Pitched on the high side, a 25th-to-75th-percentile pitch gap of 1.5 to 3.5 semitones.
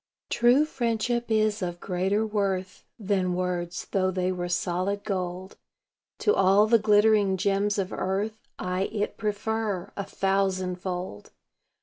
Yes: high, 195 Hz; narrow, 2.6 semitones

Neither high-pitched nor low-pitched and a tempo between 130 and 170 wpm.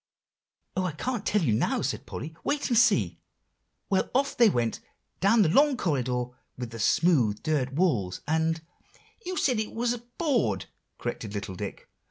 Yes: medium, 165 Hz; average, 165 wpm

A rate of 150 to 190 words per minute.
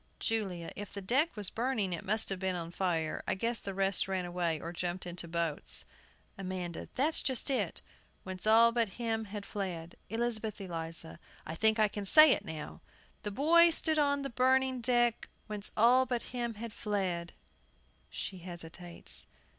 Yes: average, 175 wpm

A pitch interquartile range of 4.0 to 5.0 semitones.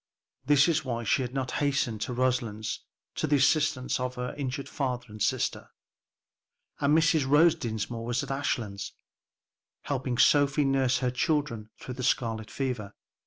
No: average, 3.1 semitones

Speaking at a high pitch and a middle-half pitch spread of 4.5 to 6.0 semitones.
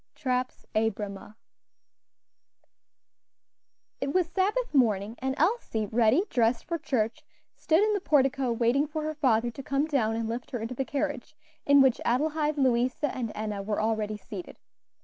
Yes: very high, 255 Hz; average, 5.1 semitones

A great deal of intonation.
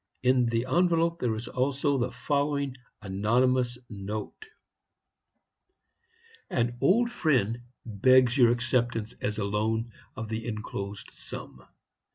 No: average, 3.3 semitones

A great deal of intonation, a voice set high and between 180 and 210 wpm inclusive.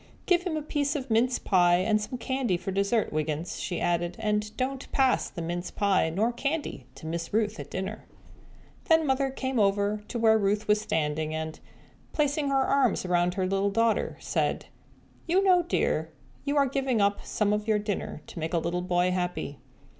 Yes: wide, 6.7 semitones; high, 210 Hz; average, 190 wpm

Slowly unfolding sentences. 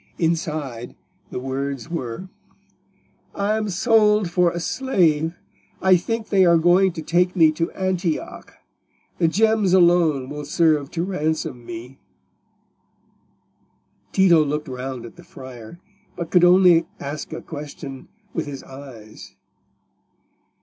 Yes: slow, 125 wpm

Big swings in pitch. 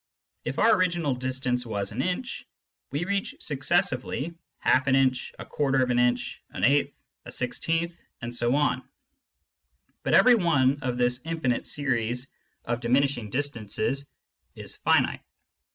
No: average, 3.7 semitones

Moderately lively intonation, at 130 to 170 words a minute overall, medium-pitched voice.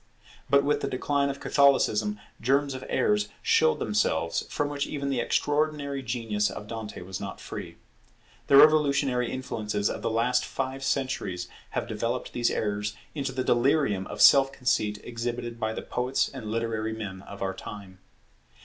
No: average, 4.6 semitones; average, 160 wpm; low, 125 Hz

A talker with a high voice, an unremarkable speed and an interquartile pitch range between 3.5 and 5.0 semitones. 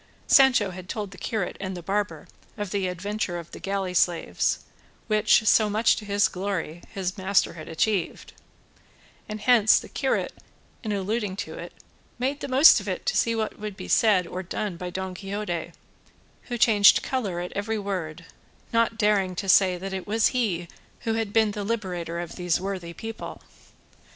No: high, 200 Hz; average, 180 wpm; average, 3.1 semitones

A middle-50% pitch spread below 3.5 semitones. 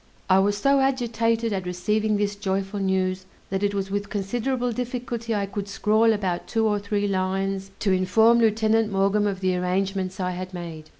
Yes: average, 2.7 semitones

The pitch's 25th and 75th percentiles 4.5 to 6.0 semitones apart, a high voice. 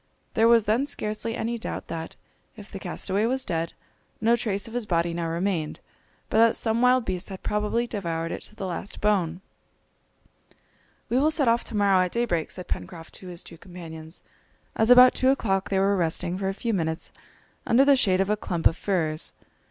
Yes: average, 4.9 semitones; high, 200 Hz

